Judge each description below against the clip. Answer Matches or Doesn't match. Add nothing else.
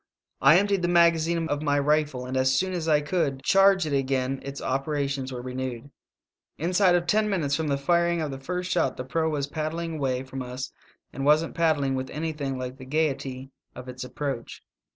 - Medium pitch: Matches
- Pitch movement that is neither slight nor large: Matches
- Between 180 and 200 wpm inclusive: Matches